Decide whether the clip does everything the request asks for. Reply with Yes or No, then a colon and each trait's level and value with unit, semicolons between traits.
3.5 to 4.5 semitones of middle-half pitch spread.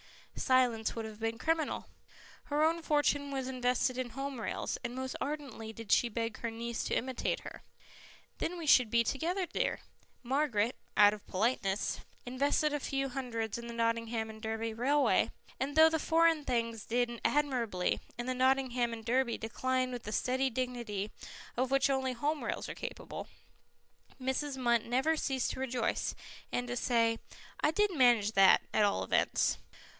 No: average, 3.0 semitones